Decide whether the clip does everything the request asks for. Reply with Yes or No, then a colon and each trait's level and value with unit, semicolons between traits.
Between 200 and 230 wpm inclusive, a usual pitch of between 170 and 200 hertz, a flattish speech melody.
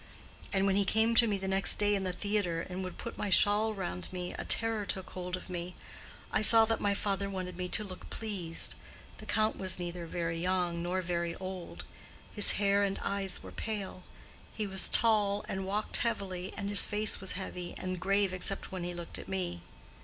Yes: fast, 205 wpm; high, 190 Hz; narrow, 2.2 semitones